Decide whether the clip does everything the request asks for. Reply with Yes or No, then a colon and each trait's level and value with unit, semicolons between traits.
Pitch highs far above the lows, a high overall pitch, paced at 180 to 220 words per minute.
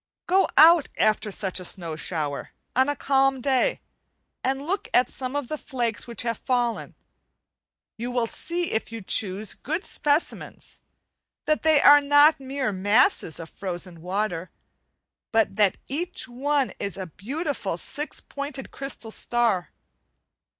No: wide, 6.2 semitones; high, 245 Hz; average, 145 wpm